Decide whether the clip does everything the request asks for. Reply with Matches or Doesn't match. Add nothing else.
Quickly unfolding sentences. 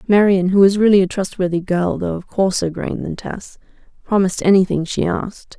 Doesn't match